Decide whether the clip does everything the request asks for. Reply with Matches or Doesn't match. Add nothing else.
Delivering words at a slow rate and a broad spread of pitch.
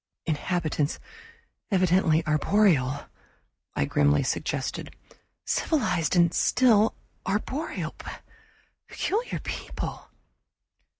Matches